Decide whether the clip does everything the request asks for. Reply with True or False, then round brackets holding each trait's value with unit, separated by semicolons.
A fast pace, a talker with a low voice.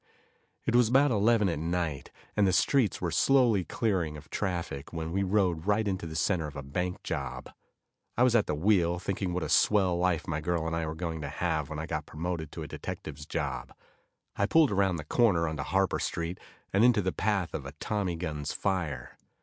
True (210 wpm; 90 Hz)